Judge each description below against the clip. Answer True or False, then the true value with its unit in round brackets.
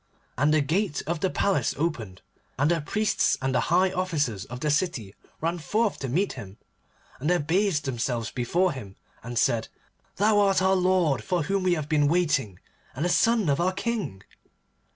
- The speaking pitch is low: False (160 Hz)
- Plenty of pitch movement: True (6.0 semitones)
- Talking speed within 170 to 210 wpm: True (185 wpm)